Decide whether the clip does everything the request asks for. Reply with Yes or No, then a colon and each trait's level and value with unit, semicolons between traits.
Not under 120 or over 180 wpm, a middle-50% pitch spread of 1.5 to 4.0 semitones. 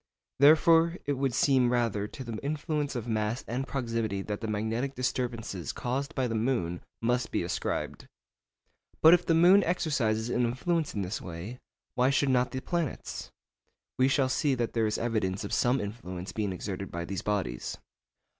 No: average, 175 wpm; average, 4.5 semitones